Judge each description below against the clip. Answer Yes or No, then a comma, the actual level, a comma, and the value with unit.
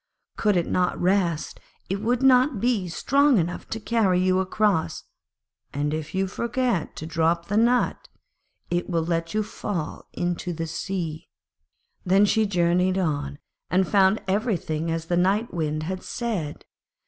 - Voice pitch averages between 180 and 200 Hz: Yes, medium, 185 Hz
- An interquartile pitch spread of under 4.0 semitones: No, average, 4.3 semitones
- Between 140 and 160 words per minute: Yes, average, 150 wpm